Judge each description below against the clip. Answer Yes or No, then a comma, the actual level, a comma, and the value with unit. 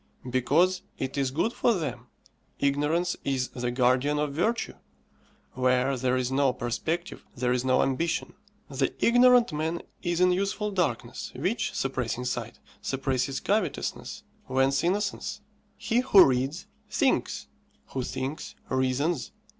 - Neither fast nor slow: No, slow, 130 wpm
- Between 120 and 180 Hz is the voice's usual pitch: Yes, medium, 140 Hz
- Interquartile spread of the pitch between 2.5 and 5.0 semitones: No, wide, 5.6 semitones